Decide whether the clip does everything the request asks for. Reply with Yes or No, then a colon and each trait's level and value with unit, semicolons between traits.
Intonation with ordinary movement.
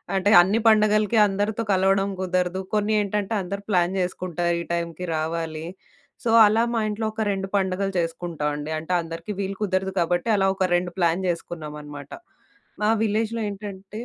Yes: average, 3.1 semitones